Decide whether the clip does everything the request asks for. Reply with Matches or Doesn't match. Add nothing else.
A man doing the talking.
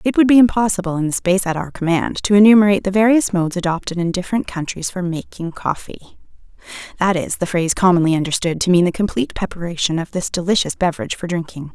Doesn't match